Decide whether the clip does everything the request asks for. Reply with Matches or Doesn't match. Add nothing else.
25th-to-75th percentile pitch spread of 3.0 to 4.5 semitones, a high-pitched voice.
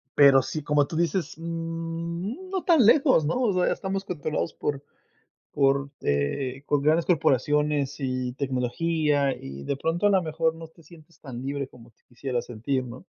Doesn't match